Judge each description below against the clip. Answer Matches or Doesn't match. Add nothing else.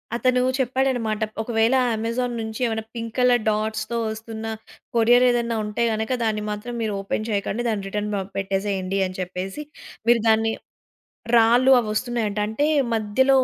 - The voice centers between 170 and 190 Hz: Doesn't match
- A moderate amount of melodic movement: Doesn't match